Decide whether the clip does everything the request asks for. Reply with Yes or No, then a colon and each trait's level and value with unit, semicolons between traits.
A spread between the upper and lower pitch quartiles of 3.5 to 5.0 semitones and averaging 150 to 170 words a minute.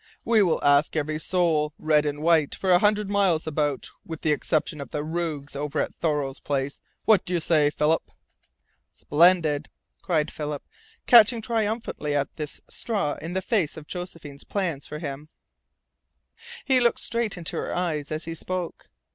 Yes: average, 3.8 semitones; average, 165 wpm